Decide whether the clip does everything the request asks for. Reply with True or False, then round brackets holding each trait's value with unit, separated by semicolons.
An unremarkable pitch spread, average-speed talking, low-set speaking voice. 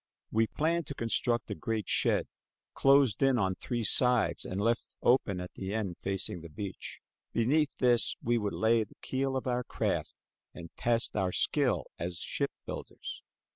True (4.4 semitones; 170 wpm; 115 Hz)